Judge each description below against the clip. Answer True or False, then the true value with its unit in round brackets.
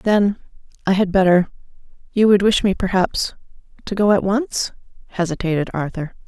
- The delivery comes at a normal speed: False (115 wpm)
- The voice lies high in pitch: True (195 Hz)